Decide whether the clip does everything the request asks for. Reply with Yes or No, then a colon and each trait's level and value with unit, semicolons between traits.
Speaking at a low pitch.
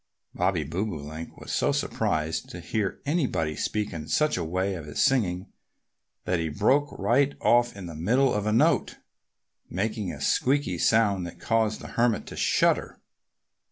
Yes: low, 100 Hz